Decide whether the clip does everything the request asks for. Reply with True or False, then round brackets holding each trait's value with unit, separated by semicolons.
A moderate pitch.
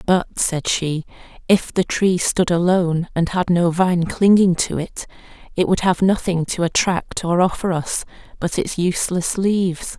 True (175 Hz)